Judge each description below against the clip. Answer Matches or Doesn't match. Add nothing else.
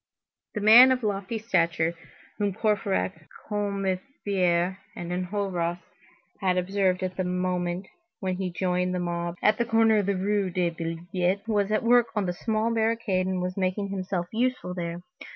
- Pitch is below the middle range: Doesn't match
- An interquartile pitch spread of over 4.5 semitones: Doesn't match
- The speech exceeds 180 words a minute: Doesn't match